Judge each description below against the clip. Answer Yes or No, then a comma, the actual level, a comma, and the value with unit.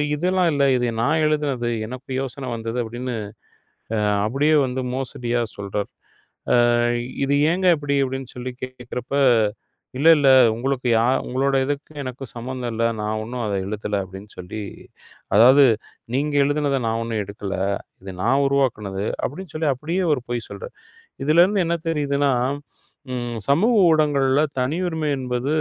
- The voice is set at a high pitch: No, low, 130 Hz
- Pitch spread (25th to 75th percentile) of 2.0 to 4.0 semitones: Yes, average, 3.6 semitones